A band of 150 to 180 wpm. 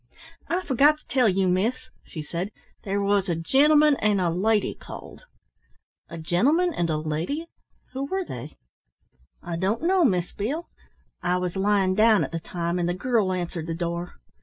Yes: average, 175 wpm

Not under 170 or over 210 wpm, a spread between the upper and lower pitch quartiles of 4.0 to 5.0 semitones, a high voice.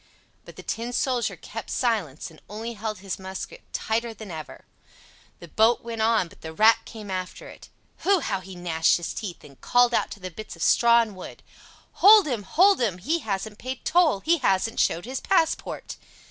Yes: average, 190 wpm; average, 4.5 semitones; high, 220 Hz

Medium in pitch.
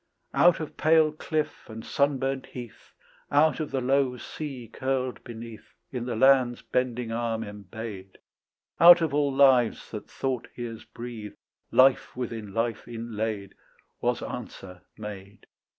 No: low, 120 Hz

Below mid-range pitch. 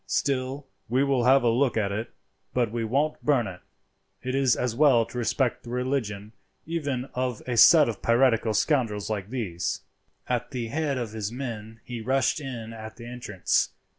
Yes: low, 120 Hz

